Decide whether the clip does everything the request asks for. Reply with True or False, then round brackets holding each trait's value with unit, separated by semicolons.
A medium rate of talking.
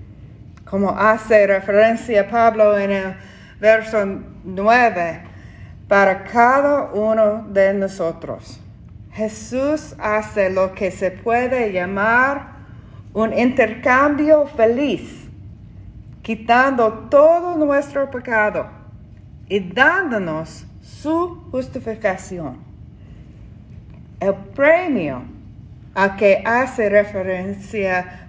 False (80 wpm)